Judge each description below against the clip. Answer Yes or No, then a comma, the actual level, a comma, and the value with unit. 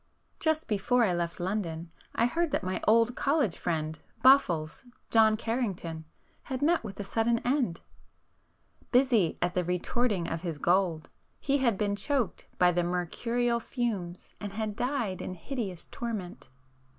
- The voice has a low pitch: No, high, 210 Hz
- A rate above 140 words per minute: Yes, average, 150 wpm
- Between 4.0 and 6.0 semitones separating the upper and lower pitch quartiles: Yes, wide, 5.6 semitones